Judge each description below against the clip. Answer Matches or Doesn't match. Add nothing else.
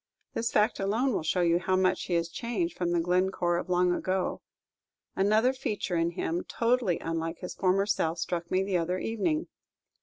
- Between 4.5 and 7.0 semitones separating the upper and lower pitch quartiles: Doesn't match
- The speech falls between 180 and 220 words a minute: Matches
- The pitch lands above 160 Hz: Matches